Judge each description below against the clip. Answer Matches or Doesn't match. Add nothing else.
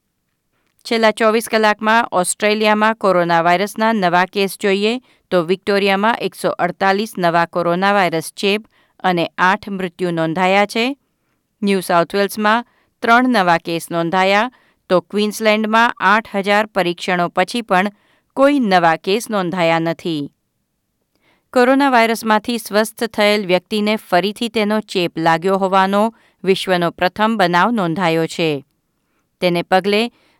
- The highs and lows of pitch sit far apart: Doesn't match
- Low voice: Doesn't match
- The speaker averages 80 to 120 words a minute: Matches